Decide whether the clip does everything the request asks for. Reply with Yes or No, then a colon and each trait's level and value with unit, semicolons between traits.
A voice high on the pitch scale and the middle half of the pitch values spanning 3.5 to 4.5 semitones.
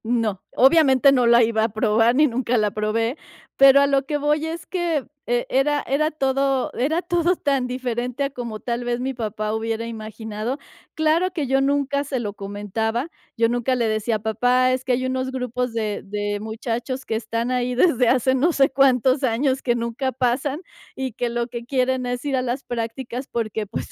No: very high, 250 Hz; average, 3.0 semitones